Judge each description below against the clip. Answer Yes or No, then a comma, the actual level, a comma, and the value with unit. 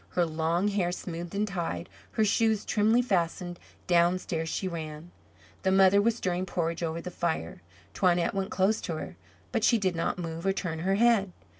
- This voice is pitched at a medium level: Yes, medium, 180 Hz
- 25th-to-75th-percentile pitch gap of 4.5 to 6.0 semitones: No, average, 2.8 semitones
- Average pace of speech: Yes, average, 180 wpm